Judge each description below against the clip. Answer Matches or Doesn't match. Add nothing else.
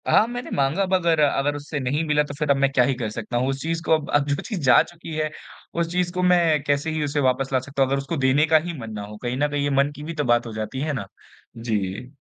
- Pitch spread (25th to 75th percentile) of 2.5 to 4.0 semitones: Matches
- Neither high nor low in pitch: Matches